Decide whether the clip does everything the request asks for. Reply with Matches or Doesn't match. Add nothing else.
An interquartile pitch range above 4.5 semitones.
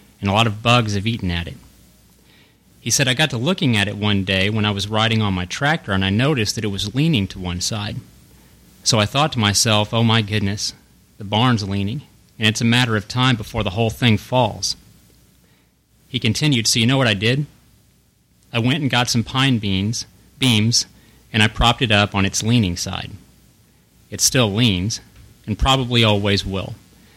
Doesn't match